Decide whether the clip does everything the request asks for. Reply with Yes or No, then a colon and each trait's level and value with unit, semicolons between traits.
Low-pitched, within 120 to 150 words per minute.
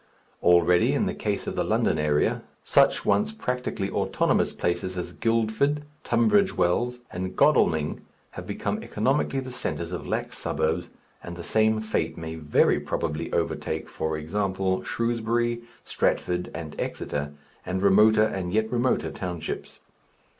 Yes: very low, 95 Hz; average, 140 wpm